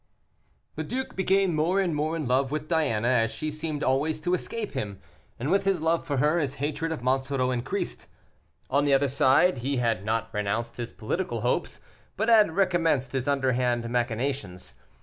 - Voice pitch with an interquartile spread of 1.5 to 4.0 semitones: No, average, 5.0 semitones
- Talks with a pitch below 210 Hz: Yes, medium, 140 Hz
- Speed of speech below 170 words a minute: No, average, 180 wpm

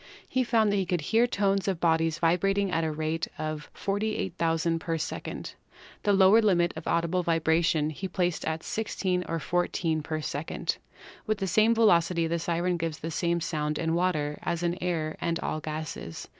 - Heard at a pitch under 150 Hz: No, medium, 170 Hz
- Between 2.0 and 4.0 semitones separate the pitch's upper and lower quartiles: Yes, average, 2.9 semitones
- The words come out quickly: No, average, 180 wpm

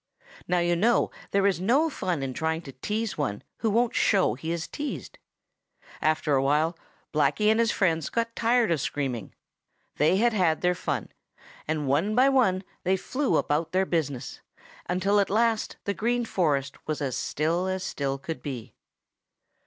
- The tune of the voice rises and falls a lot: Yes, wide, 6.2 semitones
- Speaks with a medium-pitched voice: Yes, medium, 175 Hz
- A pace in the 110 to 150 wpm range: No, average, 170 wpm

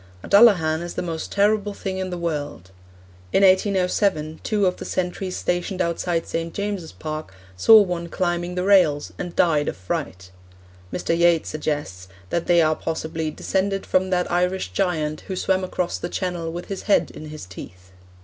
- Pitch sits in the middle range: Yes, medium, 175 Hz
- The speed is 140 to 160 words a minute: No, average, 175 wpm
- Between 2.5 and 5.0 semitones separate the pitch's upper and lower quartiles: Yes, average, 3.1 semitones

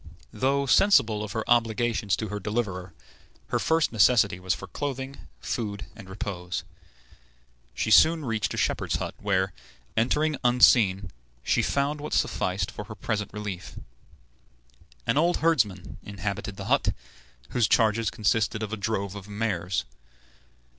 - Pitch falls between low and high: No, low, 110 Hz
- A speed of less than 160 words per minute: Yes, average, 140 wpm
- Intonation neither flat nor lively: Yes, average, 3.5 semitones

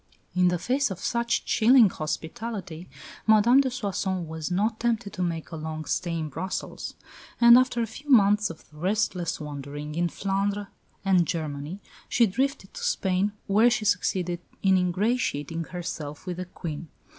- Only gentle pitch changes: No, average, 5.0 semitones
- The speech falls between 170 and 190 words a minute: No, average, 155 wpm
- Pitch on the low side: No, medium, 185 Hz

